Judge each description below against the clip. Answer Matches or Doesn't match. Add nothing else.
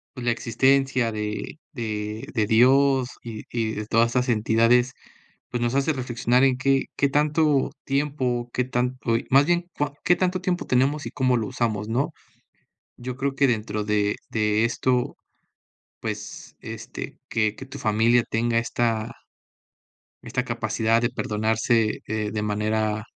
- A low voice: Matches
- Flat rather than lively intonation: Doesn't match